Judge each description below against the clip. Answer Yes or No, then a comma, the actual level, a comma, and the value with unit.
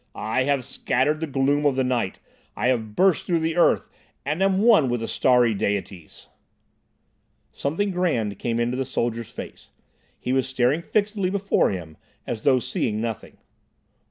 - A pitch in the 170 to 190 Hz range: No, low, 130 Hz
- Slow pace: No, average, 160 wpm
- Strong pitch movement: Yes, wide, 5.8 semitones